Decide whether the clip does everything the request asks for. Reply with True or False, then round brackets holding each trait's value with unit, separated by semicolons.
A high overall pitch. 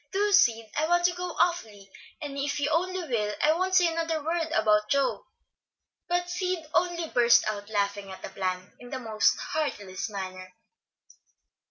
True (280 Hz)